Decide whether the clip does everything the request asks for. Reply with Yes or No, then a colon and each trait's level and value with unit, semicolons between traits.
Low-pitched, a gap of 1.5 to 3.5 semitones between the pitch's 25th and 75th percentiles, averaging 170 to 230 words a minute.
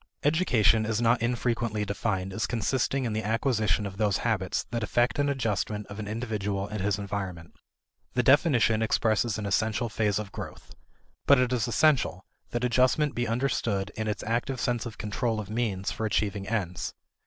Yes: low, 110 Hz; average, 2.8 semitones; average, 175 wpm